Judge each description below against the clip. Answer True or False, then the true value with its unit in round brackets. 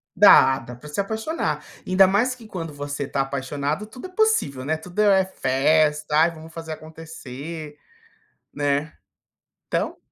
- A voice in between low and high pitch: True (155 Hz)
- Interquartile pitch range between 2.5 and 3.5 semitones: False (5.1 semitones)